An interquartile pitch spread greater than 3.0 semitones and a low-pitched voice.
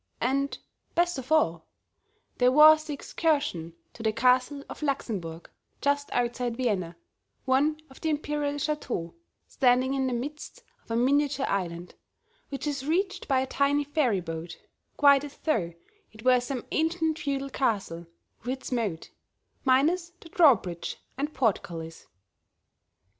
No: average, 4.7 semitones; very high, 265 Hz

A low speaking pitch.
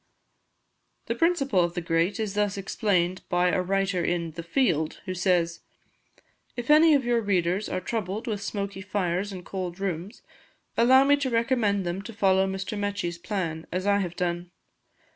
No: high, 195 Hz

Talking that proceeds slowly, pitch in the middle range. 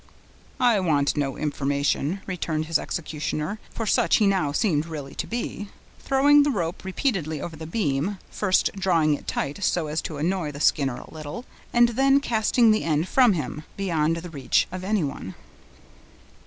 No: average, 170 wpm; medium, 170 Hz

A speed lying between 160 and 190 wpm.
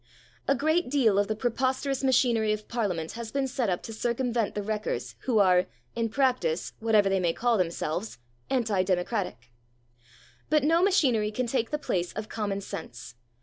Yes: average, 170 wpm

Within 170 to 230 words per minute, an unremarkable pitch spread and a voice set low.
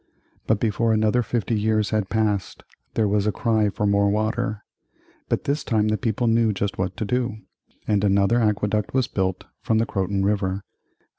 No: average, 175 wpm; narrow, 1.9 semitones; low, 105 Hz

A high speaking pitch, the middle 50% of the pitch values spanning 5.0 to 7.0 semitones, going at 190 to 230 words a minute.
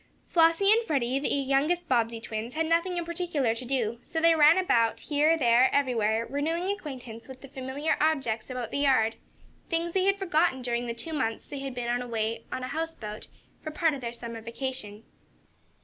Yes: very high, 270 Hz; wide, 5.6 semitones; average, 195 wpm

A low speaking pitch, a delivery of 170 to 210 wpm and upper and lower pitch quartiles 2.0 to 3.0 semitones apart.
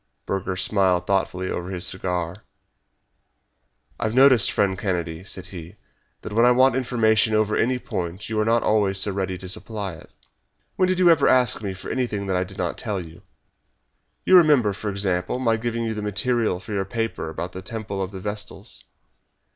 No: low, 100 Hz; average, 185 wpm; average, 3.7 semitones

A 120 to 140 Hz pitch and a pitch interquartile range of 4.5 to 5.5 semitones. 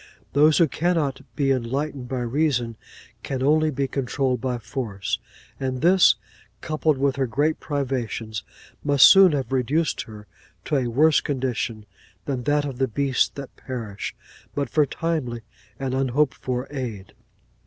No: low, 135 Hz; average, 3.0 semitones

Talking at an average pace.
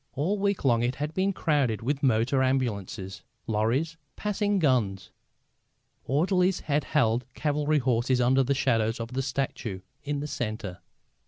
Yes: average, 145 wpm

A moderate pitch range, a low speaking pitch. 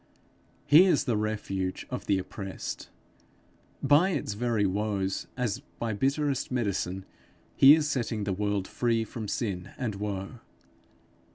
Yes: average, 4.5 semitones; low, 110 Hz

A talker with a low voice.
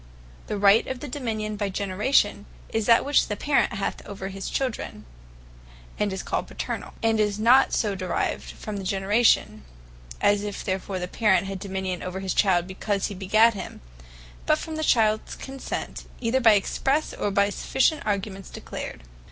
No: high, 205 Hz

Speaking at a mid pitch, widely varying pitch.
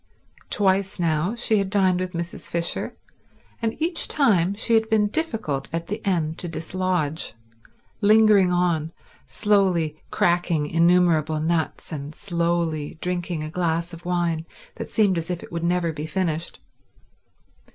No: medium, 175 Hz; average, 3.2 semitones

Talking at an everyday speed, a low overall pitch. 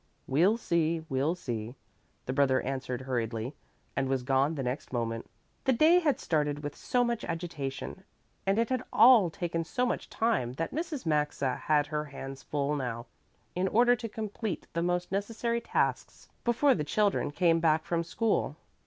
No: average, 170 wpm; medium, 165 Hz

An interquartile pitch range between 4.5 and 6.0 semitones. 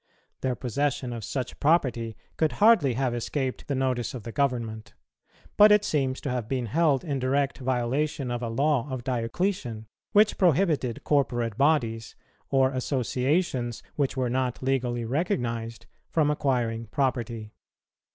No: average, 3.3 semitones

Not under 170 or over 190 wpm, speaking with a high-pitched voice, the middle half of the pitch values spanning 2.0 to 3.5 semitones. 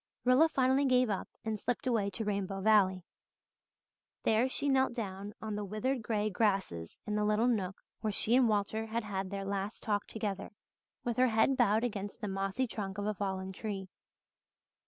Yes: average, 180 wpm; high, 210 Hz; average, 3.1 semitones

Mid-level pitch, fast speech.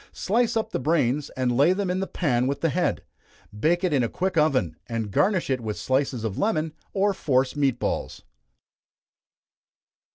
No: medium, 145 Hz; average, 180 wpm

